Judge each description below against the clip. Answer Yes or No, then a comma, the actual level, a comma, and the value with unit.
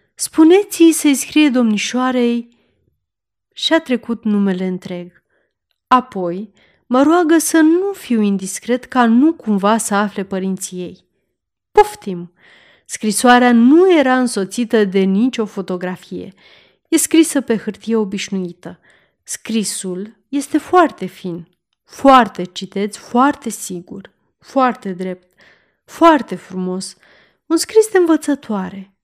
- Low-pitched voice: No, high, 225 Hz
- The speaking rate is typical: No, slow, 105 wpm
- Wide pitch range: Yes, wide, 6.8 semitones